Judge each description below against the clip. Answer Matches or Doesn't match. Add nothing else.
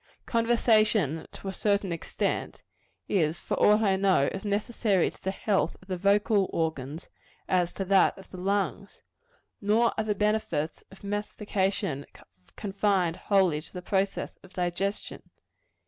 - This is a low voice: Doesn't match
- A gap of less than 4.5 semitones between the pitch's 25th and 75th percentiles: Matches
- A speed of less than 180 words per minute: Matches